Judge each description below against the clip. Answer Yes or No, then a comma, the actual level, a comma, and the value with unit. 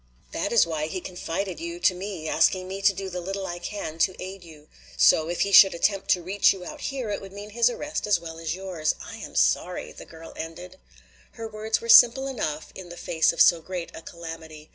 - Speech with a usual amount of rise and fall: Yes, average, 3.6 semitones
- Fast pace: Yes, fast, 230 wpm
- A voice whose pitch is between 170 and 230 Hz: Yes, medium, 185 Hz